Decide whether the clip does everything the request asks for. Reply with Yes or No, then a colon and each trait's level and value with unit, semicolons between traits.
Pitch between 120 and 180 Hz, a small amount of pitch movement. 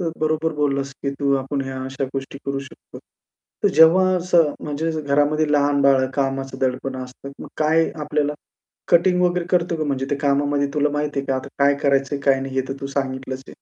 Yes: medium, 140 Hz; narrow, 2.3 semitones